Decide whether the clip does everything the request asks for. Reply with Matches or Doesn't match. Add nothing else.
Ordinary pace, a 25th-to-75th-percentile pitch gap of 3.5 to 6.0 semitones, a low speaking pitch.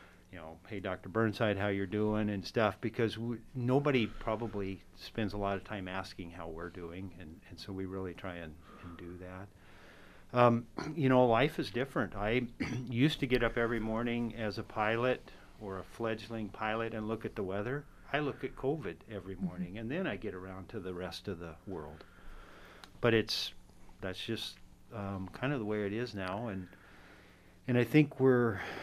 Matches